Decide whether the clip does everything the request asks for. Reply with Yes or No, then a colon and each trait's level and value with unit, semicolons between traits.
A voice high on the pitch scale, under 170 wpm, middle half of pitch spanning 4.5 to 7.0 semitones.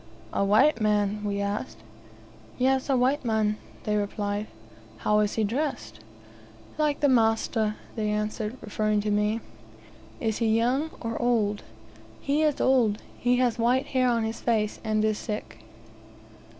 No: high, 220 Hz; average, 150 wpm; average, 2.9 semitones